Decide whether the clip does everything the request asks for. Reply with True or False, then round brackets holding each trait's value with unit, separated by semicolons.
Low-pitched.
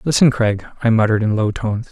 True (110 Hz)